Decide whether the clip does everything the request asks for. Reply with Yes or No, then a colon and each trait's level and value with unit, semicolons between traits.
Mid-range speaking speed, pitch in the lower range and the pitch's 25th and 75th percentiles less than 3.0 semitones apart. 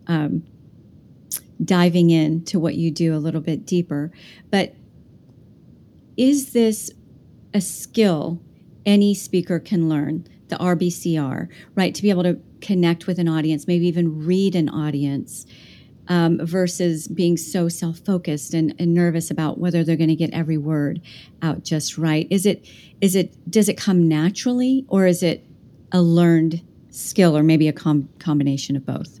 No: average, 155 wpm; medium, 170 Hz; narrow, 2.6 semitones